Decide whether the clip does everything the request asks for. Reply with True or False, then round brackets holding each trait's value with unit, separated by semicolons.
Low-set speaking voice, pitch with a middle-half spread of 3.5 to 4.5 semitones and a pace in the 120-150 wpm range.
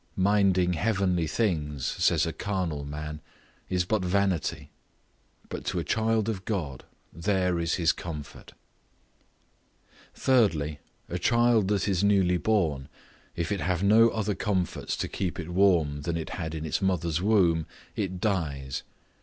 True (90 Hz; 4.0 semitones; 145 wpm)